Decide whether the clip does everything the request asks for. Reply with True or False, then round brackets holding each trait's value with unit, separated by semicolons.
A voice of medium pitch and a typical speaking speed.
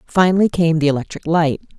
True (165 Hz; 170 wpm)